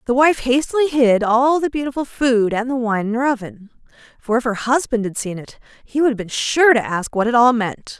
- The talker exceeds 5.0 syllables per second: Yes, 5.3 syllables/s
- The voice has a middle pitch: No, high, 245 Hz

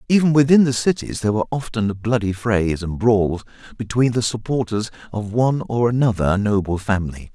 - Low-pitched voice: Yes, low, 110 Hz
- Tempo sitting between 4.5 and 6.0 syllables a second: Yes, 5.5 syllables/s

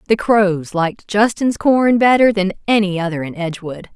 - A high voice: Yes, high, 200 Hz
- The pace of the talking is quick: No, average, 165 wpm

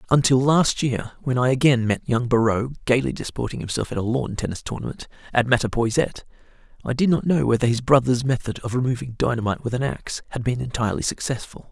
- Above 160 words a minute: Yes, average, 190 wpm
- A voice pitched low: Yes, low, 125 Hz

